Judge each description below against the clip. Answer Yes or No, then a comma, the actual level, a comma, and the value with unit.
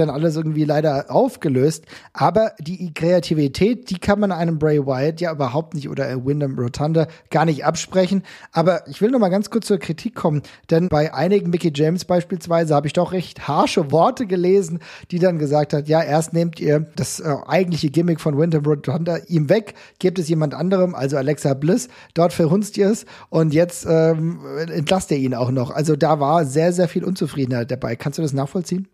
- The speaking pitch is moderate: Yes, medium, 165 Hz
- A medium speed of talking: No, fast, 195 wpm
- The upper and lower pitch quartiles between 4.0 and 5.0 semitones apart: No, average, 3.3 semitones